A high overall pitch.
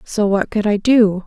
Yes: high, 210 Hz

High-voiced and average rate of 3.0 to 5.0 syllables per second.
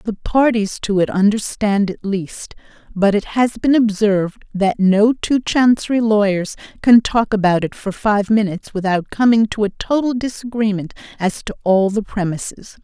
Yes: high, 210 Hz; 4.7 syllables/s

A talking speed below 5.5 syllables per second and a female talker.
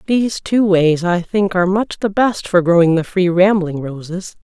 Yes: 4.8 syllables/s; female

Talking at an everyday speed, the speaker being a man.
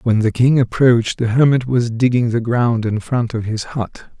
No: fast, 215 wpm; male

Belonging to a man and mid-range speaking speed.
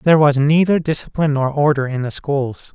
Yes: male; average, 195 wpm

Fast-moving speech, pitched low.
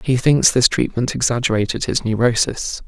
No: average, 145 wpm; low, 120 Hz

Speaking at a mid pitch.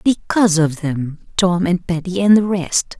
Yes: medium, 180 Hz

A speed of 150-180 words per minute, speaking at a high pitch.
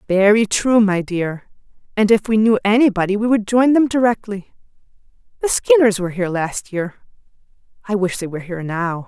Yes: average, 165 wpm; high, 205 Hz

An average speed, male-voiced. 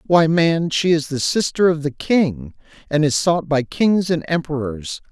Yes: average, 190 wpm; male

